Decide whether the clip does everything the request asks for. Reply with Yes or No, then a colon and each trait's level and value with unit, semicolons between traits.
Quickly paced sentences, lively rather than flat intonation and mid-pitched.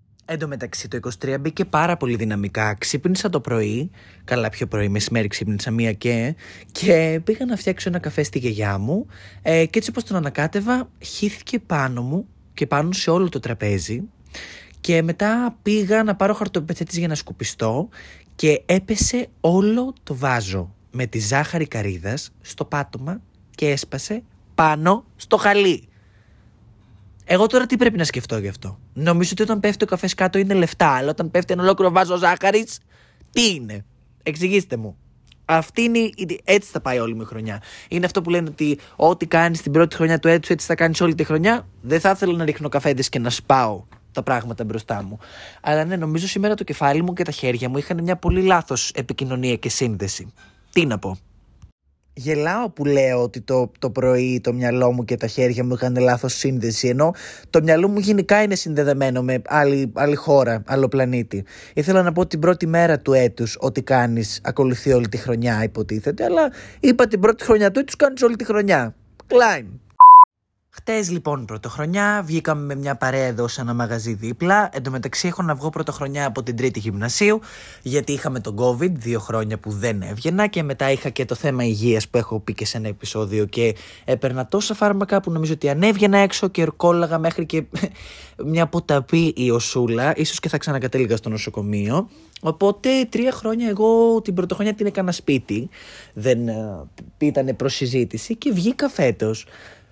Yes: fast, 180 wpm; wide, 7.4 semitones; medium, 145 Hz